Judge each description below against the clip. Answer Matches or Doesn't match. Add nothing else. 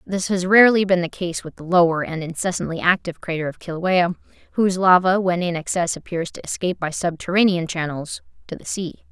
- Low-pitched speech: Doesn't match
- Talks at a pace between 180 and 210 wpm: Matches